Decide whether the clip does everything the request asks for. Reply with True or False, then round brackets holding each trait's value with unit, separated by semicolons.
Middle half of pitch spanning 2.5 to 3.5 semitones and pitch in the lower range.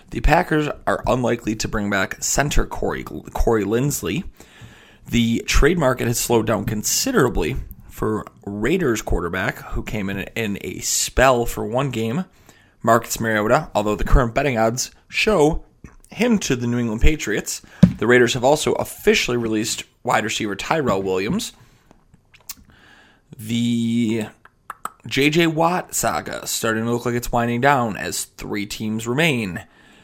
True (2.8 semitones; 115 Hz)